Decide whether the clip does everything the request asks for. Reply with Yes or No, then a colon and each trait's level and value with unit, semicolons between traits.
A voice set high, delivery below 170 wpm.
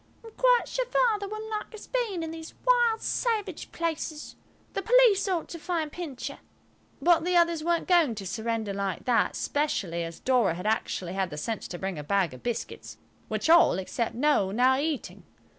No: very high, 310 Hz; average, 190 wpm